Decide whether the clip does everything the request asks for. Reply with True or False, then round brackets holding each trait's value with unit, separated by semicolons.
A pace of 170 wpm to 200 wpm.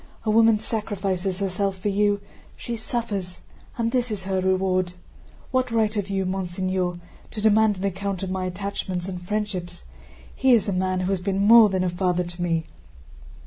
True (180 wpm)